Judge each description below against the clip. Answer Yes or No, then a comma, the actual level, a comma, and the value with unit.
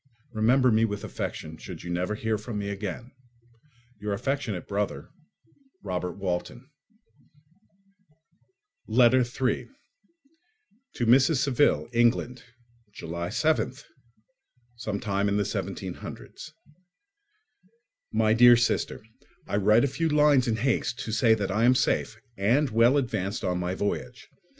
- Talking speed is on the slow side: Yes, slow, 110 wpm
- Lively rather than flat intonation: No, average, 3.8 semitones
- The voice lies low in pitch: Yes, low, 110 Hz